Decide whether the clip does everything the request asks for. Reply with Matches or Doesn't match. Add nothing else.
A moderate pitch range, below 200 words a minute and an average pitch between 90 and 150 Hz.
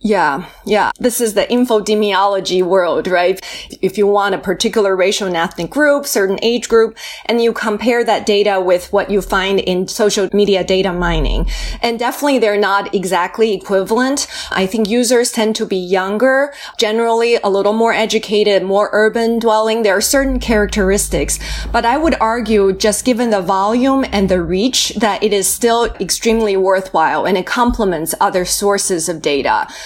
Doesn't match